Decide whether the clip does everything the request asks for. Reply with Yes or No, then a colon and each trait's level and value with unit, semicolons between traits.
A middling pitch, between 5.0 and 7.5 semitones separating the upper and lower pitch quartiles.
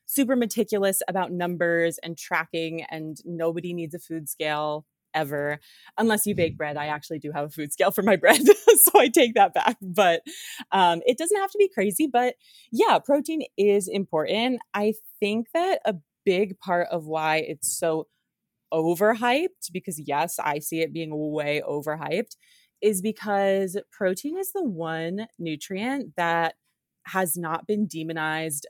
Yes: medium, 180 Hz; average, 5.3 semitones